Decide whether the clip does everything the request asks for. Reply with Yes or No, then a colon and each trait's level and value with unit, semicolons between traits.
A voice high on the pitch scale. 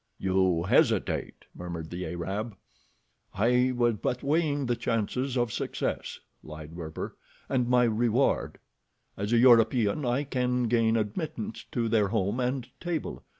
No: low, 120 Hz